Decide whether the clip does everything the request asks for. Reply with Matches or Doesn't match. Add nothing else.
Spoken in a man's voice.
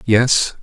Matches